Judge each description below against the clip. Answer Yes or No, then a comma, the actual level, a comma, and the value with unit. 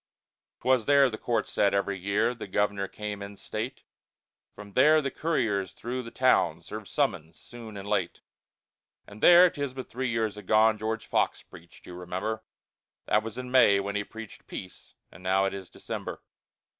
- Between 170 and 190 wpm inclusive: Yes, average, 175 wpm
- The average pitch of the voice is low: Yes, low, 110 Hz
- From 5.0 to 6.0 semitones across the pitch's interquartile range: No, average, 3.8 semitones